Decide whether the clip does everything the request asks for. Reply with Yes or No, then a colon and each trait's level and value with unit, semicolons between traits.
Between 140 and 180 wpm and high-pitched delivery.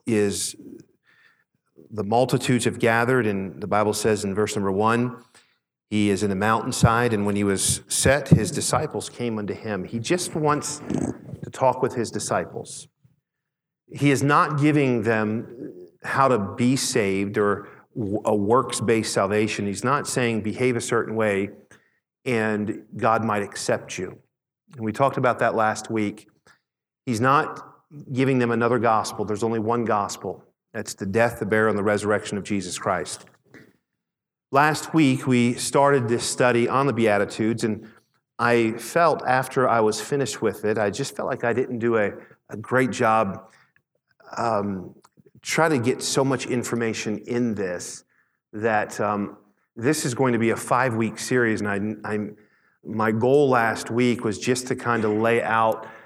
No: average, 165 wpm; low, 115 Hz